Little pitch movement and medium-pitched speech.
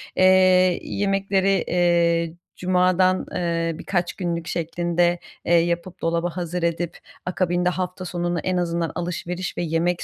Yes: narrow, 1.3 semitones; medium, 175 Hz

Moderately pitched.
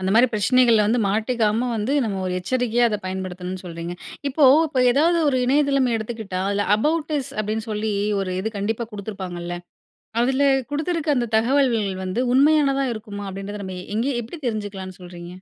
No: high, 220 Hz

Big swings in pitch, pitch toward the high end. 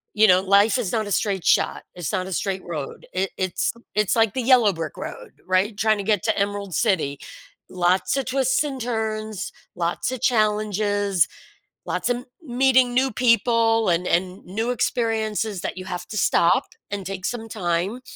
No: average, 3.7 semitones; high, 210 Hz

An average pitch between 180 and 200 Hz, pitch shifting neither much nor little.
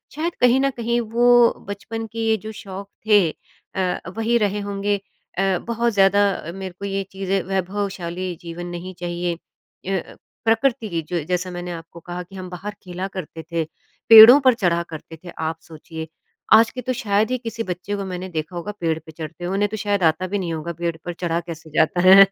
Yes: high, 190 Hz; average, 3.7 semitones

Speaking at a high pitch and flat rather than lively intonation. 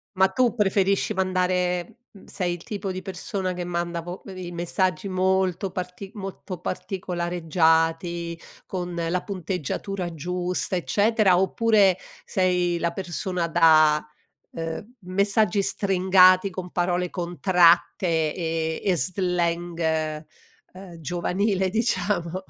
No: medium, 180 Hz; narrow, 1.8 semitones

